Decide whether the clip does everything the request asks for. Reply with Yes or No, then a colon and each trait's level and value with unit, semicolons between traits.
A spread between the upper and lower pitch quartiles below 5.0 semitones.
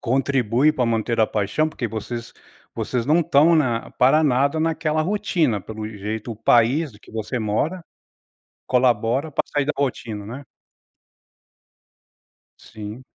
No: average, 5.3 semitones